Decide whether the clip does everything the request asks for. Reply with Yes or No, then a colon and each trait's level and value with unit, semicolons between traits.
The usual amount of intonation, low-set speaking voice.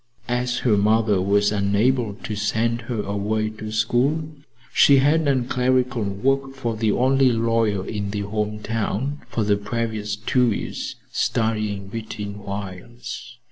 Yes: average, 3.1 semitones; low, 110 Hz